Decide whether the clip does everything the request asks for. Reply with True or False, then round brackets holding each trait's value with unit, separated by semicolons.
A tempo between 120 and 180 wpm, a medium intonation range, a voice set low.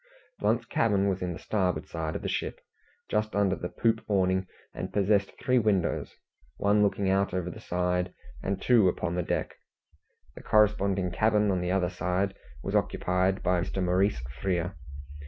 False (165 wpm; 2.2 semitones; 95 Hz)